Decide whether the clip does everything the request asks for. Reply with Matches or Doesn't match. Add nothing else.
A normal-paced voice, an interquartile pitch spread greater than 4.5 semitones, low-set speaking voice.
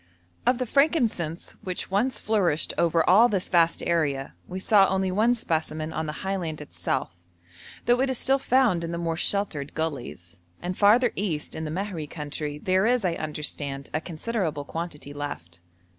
Doesn't match